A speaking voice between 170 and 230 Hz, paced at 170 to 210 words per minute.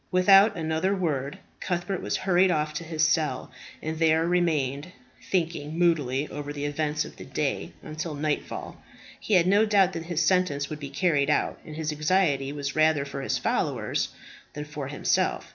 No: medium, 155 Hz; average, 175 wpm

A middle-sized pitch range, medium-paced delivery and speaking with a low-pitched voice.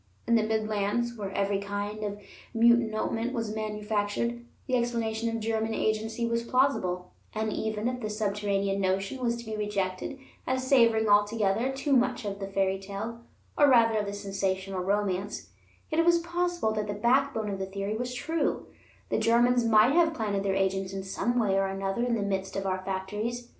No: average, 3.1 semitones; average, 180 wpm; high, 215 Hz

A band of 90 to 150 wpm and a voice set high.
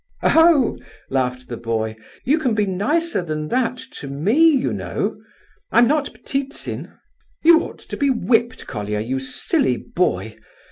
Yes: average, 140 wpm; high, 235 Hz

